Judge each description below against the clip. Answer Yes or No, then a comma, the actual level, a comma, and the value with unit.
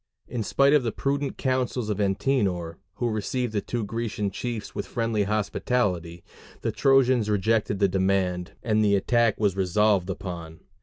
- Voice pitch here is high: No, low, 105 Hz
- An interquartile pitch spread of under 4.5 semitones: Yes, average, 3.7 semitones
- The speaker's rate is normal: Yes, average, 155 wpm